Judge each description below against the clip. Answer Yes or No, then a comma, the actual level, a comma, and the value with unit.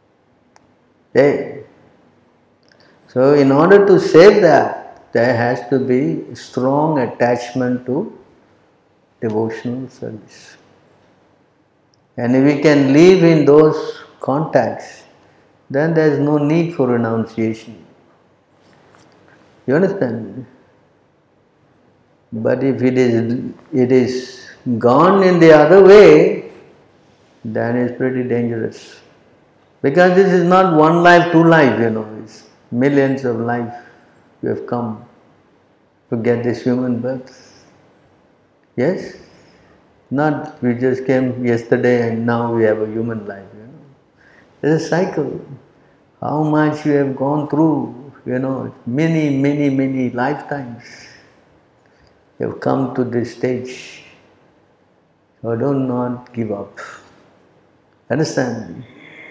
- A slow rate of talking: Yes, slow, 115 wpm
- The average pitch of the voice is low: Yes, low, 130 Hz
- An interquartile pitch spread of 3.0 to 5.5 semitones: Yes, average, 3.8 semitones